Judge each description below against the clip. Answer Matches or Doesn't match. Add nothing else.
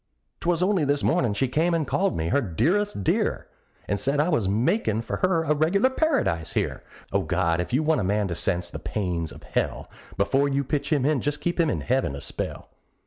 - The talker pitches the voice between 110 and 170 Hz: Matches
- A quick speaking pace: Matches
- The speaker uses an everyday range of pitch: Doesn't match